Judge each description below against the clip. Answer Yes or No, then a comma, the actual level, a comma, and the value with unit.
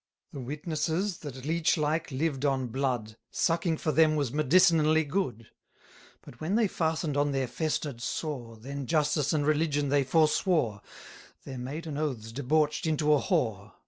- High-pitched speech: No, medium, 150 Hz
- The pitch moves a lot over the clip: No, average, 3.4 semitones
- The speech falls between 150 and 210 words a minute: Yes, average, 155 wpm